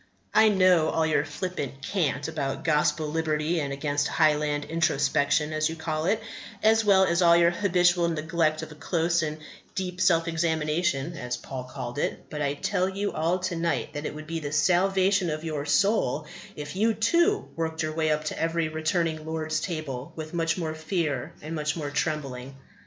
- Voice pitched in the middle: Yes, medium, 160 Hz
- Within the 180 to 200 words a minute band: Yes, average, 185 wpm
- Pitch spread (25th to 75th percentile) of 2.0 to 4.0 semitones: Yes, narrow, 2.4 semitones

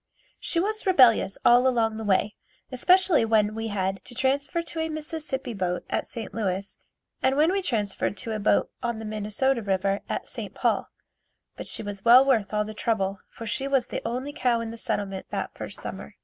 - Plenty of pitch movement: No, average, 4.5 semitones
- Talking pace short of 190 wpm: No, average, 200 wpm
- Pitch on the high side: Yes, high, 230 Hz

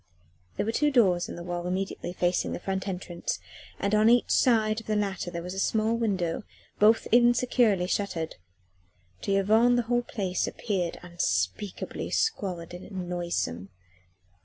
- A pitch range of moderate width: Yes, average, 4.0 semitones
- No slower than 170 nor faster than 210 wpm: No, average, 155 wpm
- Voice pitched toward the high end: Yes, high, 195 Hz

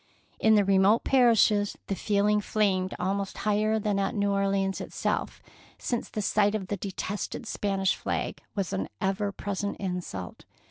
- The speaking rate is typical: Yes, average, 165 wpm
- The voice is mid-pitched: No, high, 200 Hz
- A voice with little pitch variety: Yes, narrow, 1.5 semitones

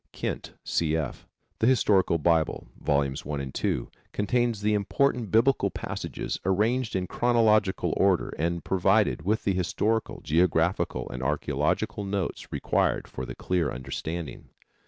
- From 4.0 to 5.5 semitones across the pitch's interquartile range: Yes, average, 5.0 semitones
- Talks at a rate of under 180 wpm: Yes, slow, 135 wpm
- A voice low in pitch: Yes, very low, 95 Hz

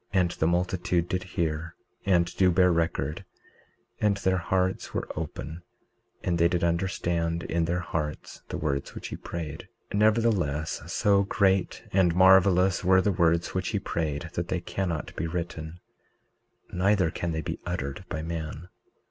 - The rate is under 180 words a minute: Yes, average, 160 wpm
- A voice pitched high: No, very low, 85 Hz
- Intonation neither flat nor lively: No, narrow, 2.3 semitones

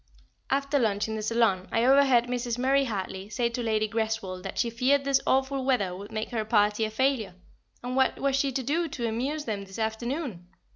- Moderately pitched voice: No, high, 235 Hz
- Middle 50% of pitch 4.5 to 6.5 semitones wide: No, average, 3.7 semitones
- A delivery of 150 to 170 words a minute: No, fast, 205 wpm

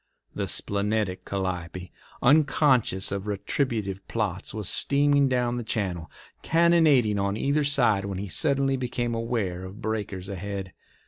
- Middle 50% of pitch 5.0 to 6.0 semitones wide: Yes, average, 5.3 semitones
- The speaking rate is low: Yes, slow, 130 wpm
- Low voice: Yes, low, 110 Hz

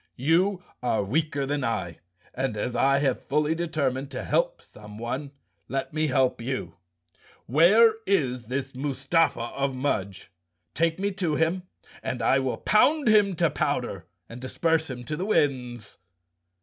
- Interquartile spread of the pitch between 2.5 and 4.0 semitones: No, average, 4.8 semitones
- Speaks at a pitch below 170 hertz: Yes, medium, 140 Hz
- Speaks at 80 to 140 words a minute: No, average, 150 wpm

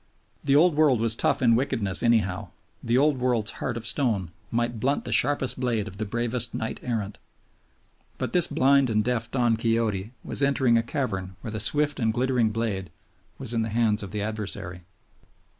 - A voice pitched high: No, low, 115 Hz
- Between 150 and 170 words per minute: No, average, 185 wpm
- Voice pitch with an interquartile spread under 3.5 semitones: Yes, average, 3.0 semitones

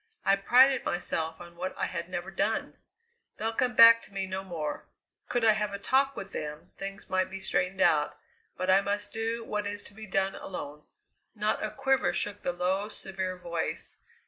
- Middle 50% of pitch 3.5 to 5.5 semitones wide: No, average, 3.0 semitones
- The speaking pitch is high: Yes, high, 195 Hz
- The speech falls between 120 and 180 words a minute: No, average, 195 wpm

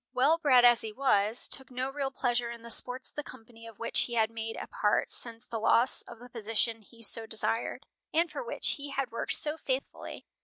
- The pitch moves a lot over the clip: No, average, 2.8 semitones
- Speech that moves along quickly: Yes, fast, 225 wpm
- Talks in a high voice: Yes, high, 240 Hz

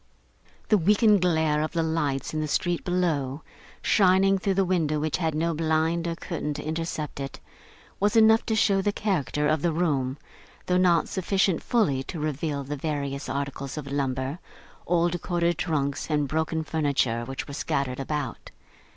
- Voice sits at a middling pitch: Yes, medium, 160 Hz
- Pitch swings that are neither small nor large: Yes, average, 3.8 semitones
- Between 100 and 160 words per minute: No, average, 170 wpm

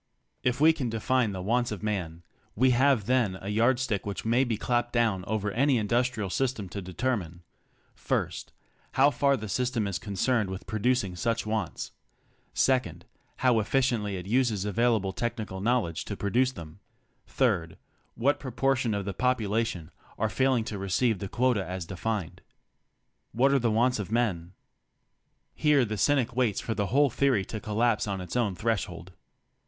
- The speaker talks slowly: No, average, 160 wpm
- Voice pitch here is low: Yes, low, 110 Hz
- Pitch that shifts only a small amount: No, average, 4.1 semitones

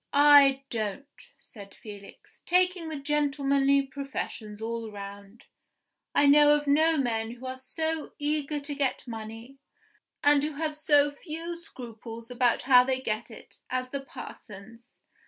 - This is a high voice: Yes, very high, 270 Hz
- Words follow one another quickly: No, average, 140 wpm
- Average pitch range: Yes, average, 4.4 semitones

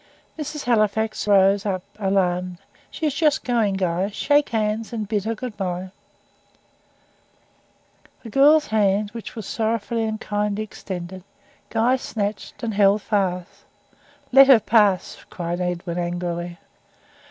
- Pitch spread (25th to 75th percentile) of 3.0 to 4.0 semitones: Yes, average, 3.4 semitones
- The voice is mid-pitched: No, high, 210 Hz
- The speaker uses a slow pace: Yes, slow, 130 wpm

